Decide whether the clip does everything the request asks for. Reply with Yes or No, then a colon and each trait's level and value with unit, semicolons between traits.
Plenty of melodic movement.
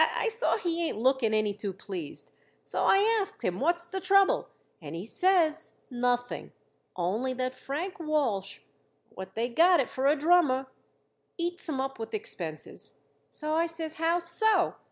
Yes: wide, 7.2 semitones